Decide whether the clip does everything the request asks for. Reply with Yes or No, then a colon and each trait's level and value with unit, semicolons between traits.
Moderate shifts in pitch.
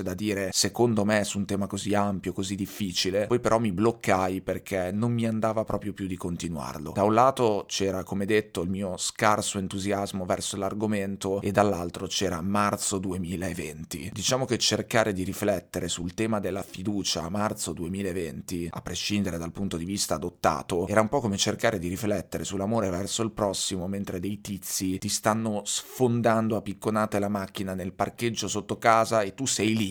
No: narrow, 2.2 semitones